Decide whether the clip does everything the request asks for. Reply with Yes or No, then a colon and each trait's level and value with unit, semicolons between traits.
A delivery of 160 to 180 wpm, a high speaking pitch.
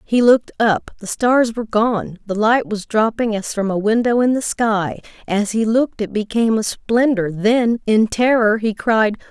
No: average, 195 wpm; high, 220 Hz